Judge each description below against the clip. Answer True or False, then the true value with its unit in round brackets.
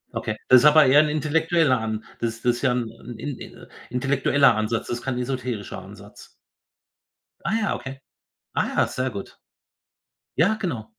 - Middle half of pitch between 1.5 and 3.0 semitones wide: False (4.1 semitones)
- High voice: False (130 Hz)